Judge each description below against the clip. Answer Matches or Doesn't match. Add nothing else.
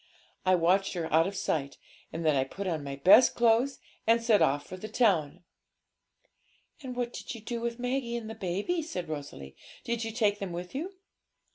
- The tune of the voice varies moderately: Doesn't match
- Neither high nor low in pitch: Doesn't match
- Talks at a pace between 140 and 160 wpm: Doesn't match